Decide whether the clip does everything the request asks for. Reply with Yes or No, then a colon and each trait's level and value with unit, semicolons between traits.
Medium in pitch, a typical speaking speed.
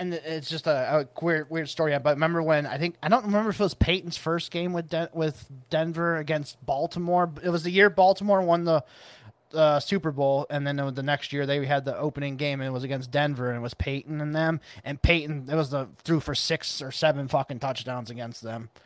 No: medium, 155 Hz; fast, 235 wpm